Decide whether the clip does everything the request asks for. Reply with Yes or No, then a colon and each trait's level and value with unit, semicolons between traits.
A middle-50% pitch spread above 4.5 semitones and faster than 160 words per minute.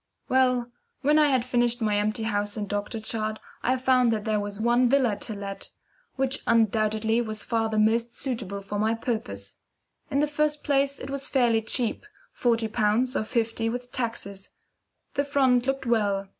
No: average, 3.1 semitones; average, 175 wpm